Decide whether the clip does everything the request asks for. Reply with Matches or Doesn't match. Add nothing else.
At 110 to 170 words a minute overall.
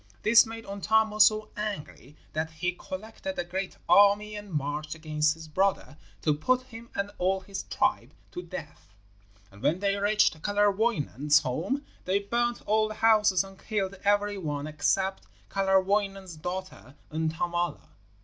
Matches